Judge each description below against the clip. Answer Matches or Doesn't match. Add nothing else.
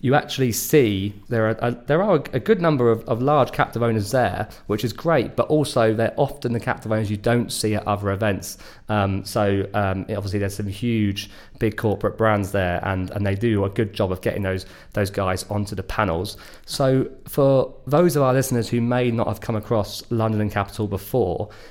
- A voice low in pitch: Matches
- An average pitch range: Matches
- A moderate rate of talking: Doesn't match